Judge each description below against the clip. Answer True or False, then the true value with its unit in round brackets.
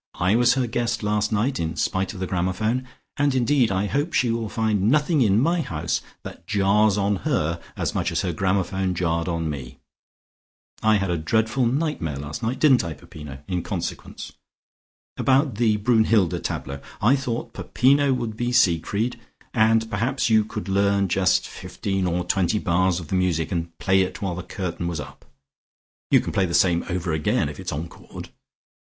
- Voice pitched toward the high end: False (100 Hz)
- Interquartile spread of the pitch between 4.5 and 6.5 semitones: True (5.1 semitones)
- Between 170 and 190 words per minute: True (185 wpm)